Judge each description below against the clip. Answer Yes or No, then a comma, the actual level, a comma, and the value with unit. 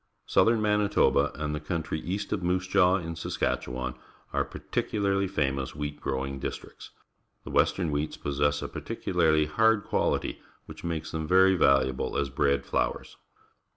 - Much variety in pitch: No, average, 4.8 semitones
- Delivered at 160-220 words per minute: No, average, 145 wpm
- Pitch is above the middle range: No, very low, 80 Hz